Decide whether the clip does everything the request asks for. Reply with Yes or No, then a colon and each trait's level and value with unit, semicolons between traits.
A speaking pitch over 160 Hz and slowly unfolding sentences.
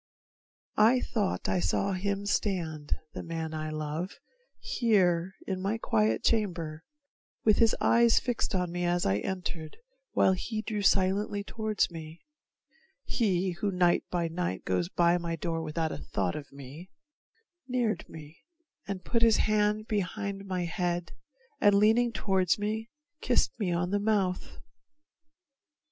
No: medium, 185 Hz; average, 145 wpm